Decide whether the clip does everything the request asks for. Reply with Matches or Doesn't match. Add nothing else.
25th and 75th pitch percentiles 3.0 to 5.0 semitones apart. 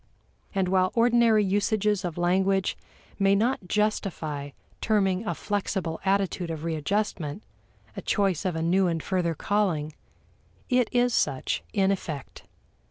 Matches